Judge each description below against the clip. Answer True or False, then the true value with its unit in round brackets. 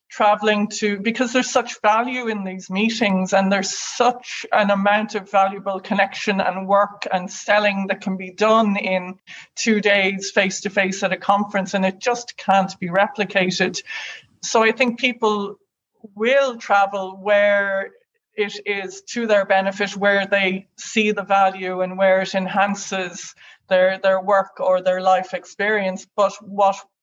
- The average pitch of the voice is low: False (200 Hz)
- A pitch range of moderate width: False (1.7 semitones)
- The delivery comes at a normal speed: True (155 wpm)